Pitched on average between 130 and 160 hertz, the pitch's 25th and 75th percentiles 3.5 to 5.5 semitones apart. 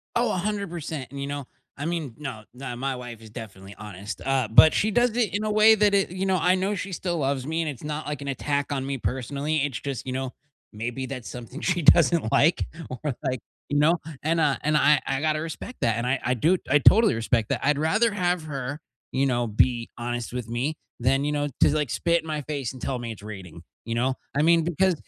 Yes: medium, 140 Hz; average, 5.0 semitones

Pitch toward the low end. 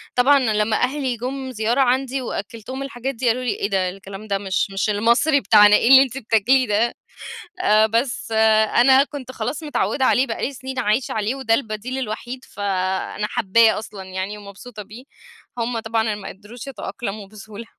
No: high, 230 Hz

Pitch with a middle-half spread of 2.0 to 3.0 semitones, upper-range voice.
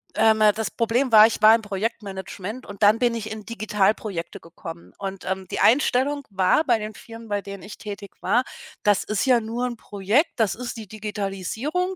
Yes: average, 2.7 semitones; high, 215 Hz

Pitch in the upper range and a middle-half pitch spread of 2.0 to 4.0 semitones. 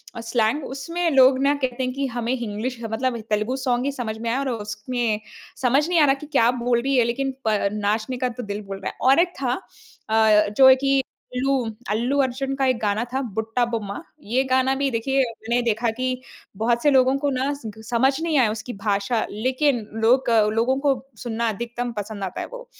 Yes: high, 245 Hz; average, 3.2 semitones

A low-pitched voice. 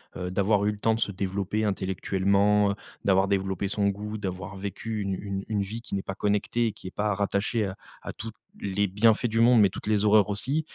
Yes: low, 100 Hz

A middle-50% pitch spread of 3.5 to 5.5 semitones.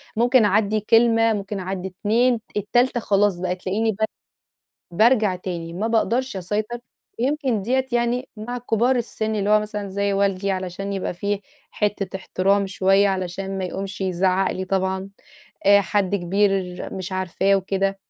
No: average, 2.7 semitones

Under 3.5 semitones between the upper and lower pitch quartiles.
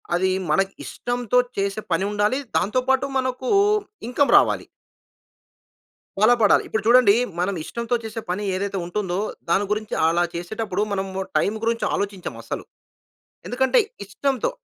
No: average, 4.1 semitones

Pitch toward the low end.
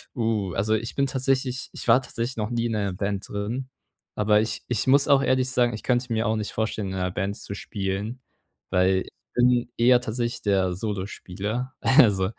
Yes: low, 110 Hz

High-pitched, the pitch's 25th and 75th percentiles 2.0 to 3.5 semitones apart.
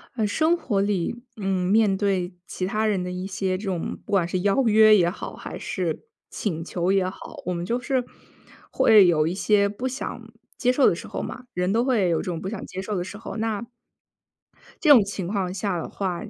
Yes: high, 195 Hz; average, 3.2 semitones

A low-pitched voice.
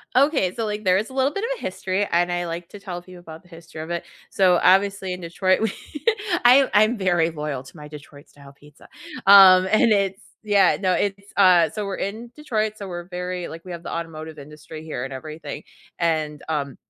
No: medium, 180 Hz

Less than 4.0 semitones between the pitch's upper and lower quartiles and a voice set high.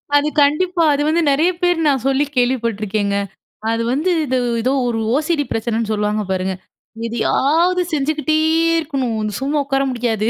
No: average, 5.3 semitones; very high, 270 Hz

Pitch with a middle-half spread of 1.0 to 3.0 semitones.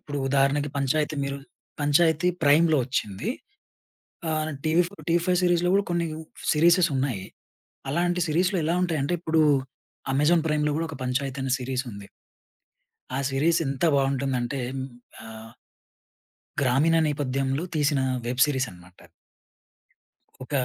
No: average, 3.7 semitones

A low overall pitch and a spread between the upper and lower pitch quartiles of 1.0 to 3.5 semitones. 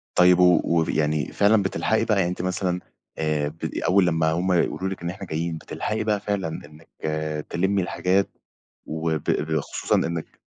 Yes: very low, 90 Hz; average, 3.2 semitones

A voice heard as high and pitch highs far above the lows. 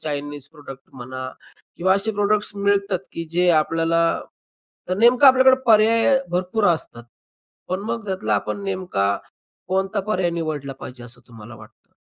No: medium, 180 Hz; wide, 6.2 semitones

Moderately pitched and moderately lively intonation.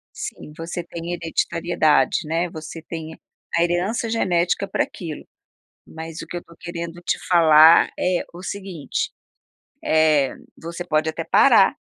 No: medium, 170 Hz; narrow, 1.7 semitones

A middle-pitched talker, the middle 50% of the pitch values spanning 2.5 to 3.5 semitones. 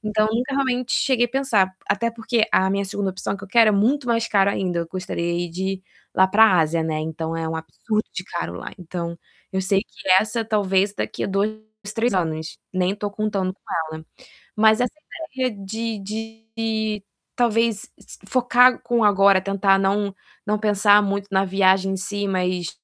No: high, 200 Hz; average, 2.9 semitones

